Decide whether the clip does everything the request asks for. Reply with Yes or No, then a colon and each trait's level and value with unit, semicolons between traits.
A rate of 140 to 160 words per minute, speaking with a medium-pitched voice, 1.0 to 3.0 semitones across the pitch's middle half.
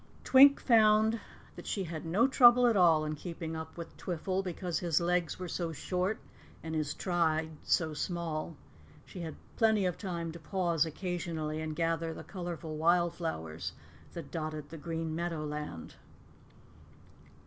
Yes: average, 150 wpm; medium, 170 Hz; narrow, 2.4 semitones